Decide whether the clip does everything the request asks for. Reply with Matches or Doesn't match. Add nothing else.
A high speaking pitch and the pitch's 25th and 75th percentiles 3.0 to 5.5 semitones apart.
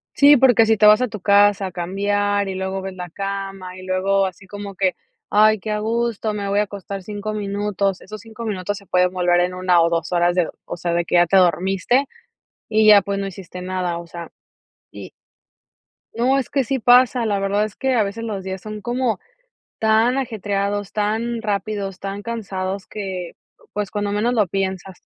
Doesn't match